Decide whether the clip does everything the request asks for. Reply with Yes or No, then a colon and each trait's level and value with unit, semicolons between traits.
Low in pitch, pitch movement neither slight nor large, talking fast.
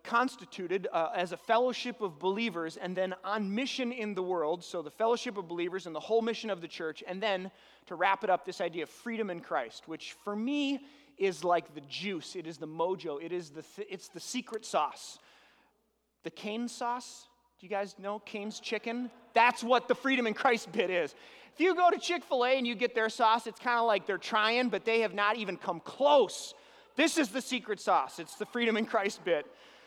No: high, 215 Hz; average, 4.6 semitones; fast, 220 wpm